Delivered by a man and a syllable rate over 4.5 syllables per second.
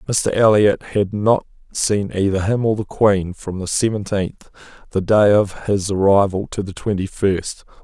No: male; 4.2 syllables/s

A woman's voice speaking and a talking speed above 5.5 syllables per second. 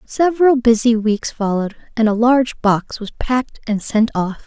No: female; 4.9 syllables/s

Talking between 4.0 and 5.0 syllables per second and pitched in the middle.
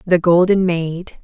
No: 3.7 syllables/s; medium, 175 Hz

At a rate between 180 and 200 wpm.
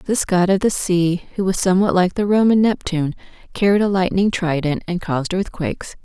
Yes: average, 190 wpm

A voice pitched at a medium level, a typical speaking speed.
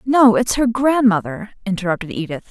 No: high, 215 Hz; average, 145 wpm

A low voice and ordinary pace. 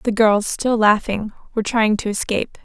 No: high, 215 Hz; average, 180 wpm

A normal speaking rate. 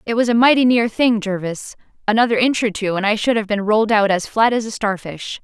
No: fast, 255 wpm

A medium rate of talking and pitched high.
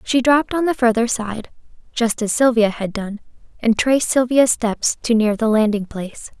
Yes: average, 190 wpm; high, 230 Hz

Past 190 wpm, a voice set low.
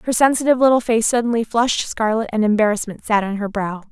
No: average, 200 wpm; high, 225 Hz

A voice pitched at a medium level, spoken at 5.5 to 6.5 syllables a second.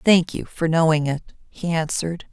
No: medium, 165 Hz; 5.0 syllables/s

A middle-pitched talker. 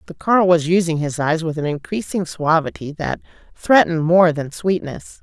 Yes: medium, 165 Hz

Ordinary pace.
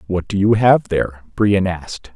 Yes: average, 195 wpm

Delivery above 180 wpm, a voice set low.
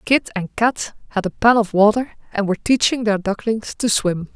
No: fast, 205 wpm; high, 215 Hz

